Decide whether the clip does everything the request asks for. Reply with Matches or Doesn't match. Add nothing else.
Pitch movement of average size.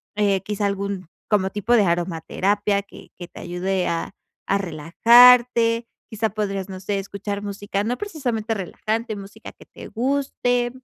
Matches